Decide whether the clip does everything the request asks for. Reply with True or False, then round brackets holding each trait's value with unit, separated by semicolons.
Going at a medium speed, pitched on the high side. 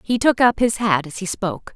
False (275 wpm; 205 Hz)